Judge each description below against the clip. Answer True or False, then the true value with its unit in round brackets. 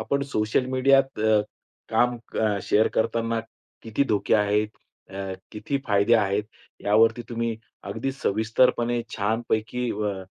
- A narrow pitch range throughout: True (2.3 semitones)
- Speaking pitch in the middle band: False (110 Hz)